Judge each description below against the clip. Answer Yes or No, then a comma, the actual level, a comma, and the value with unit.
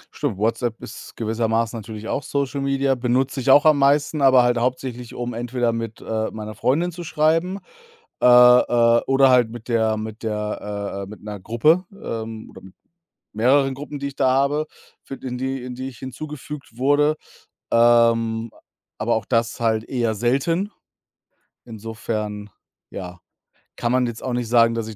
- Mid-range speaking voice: No, low, 120 Hz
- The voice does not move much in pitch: No, average, 3.2 semitones